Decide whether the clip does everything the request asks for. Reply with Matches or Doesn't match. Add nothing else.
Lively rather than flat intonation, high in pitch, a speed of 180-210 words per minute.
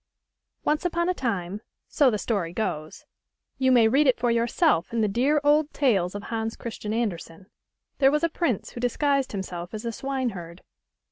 Matches